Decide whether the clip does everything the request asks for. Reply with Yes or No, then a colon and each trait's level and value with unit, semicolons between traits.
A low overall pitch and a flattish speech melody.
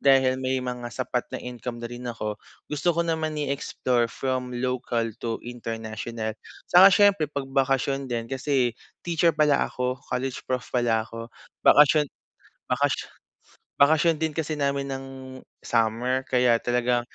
No: low, 130 Hz; average, 3.0 semitones